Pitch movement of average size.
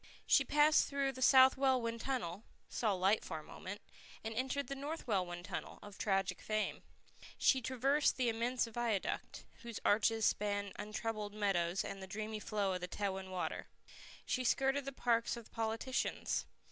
Yes: average, 4.5 semitones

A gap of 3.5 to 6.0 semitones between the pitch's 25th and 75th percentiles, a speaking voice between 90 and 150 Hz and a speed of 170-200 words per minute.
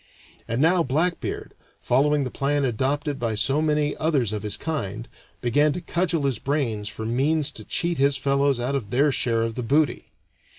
Yes: average, 4.1 semitones; medium, 140 Hz; average, 180 wpm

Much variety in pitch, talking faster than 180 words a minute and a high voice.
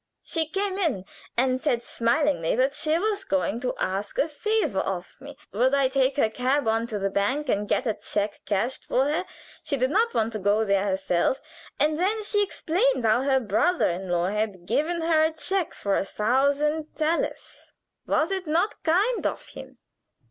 Yes: wide, 7.2 semitones; average, 190 wpm; very high, 265 Hz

